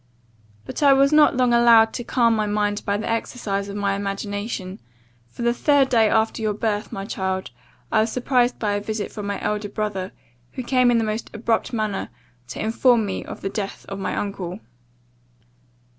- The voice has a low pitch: No, high, 215 Hz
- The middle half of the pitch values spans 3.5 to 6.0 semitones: No, average, 2.8 semitones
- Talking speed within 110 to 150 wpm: No, average, 190 wpm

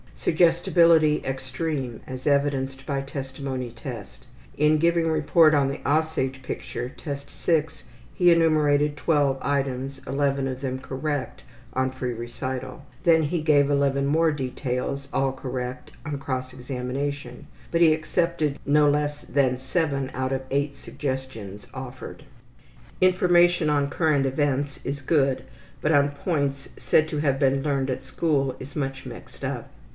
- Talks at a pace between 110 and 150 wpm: Yes, average, 140 wpm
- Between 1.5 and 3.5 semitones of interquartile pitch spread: Yes, narrow, 2.5 semitones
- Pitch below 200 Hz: Yes, medium, 140 Hz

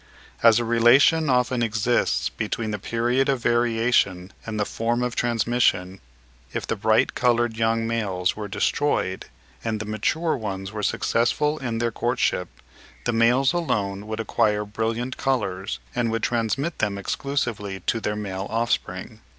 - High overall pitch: No, low, 115 Hz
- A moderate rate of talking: Yes, average, 150 wpm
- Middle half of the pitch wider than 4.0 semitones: No, narrow, 2.6 semitones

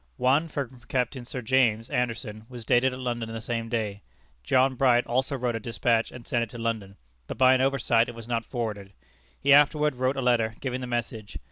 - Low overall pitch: Yes, low, 120 Hz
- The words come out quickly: Yes, fast, 210 wpm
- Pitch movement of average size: No, narrow, 2.3 semitones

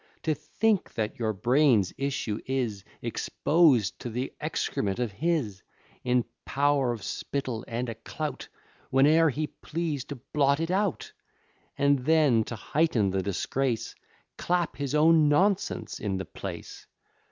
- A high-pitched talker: No, low, 135 Hz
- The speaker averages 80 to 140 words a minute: Yes, slow, 135 wpm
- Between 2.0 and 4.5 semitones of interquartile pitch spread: No, average, 5.2 semitones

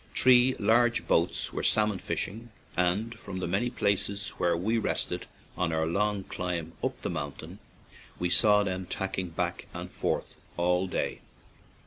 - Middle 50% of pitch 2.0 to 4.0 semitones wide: Yes, average, 3.3 semitones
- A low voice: Yes, very low, 95 Hz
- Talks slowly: No, average, 150 wpm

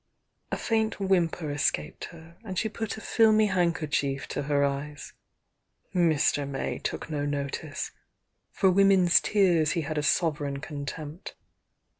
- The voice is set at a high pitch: No, medium, 160 Hz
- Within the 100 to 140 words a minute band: Yes, slow, 135 wpm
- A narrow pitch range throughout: No, average, 4.7 semitones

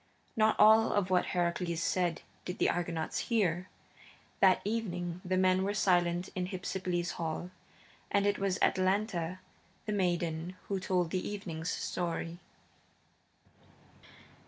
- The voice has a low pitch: No, medium, 180 Hz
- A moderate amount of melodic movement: No, narrow, 2.2 semitones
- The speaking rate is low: Yes, slow, 125 wpm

